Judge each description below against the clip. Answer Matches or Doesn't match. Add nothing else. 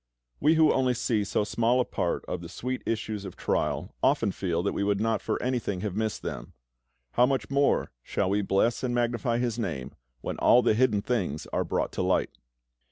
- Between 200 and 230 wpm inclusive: Matches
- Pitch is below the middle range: Matches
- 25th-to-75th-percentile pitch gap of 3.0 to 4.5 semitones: Matches